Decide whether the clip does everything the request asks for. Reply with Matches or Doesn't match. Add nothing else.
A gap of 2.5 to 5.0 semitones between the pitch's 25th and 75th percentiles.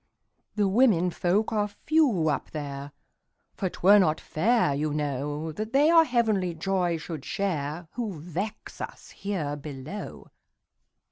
Doesn't match